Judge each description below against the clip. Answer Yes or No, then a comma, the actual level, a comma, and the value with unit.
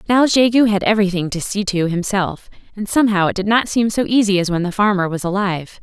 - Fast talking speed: Yes, fast, 225 wpm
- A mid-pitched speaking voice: No, high, 200 Hz